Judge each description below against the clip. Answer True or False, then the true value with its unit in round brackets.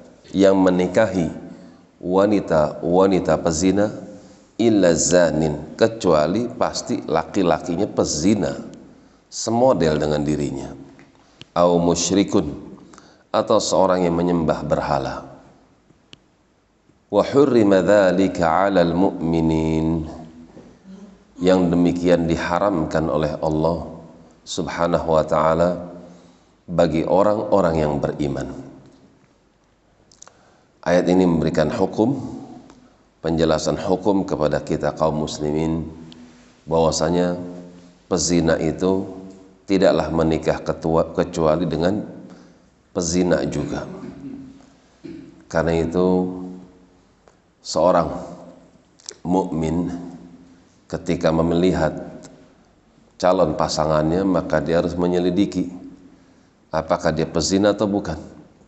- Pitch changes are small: True (2.2 semitones)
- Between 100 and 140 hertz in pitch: False (85 Hz)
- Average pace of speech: False (70 wpm)